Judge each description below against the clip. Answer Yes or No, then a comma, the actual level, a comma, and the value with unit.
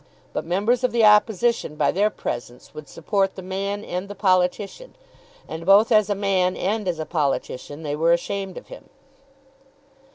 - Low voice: No, high, 195 Hz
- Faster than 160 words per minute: Yes, average, 170 wpm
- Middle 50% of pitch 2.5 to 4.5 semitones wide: Yes, average, 3.5 semitones